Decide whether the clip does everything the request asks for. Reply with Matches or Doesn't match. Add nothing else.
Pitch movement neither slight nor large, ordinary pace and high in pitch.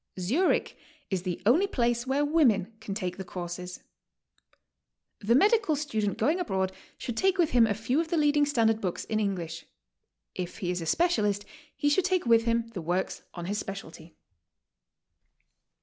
Doesn't match